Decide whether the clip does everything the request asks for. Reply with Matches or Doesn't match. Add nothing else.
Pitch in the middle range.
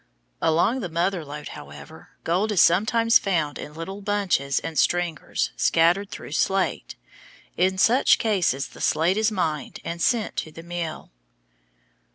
Matches